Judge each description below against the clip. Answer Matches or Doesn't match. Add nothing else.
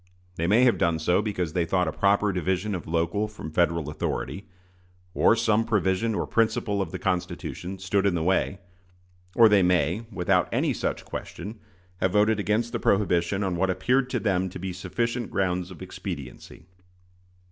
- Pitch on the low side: Matches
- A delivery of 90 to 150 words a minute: Doesn't match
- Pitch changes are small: Doesn't match